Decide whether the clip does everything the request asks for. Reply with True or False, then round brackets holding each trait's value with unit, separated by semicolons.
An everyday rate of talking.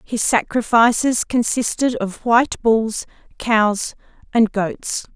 False (105 wpm)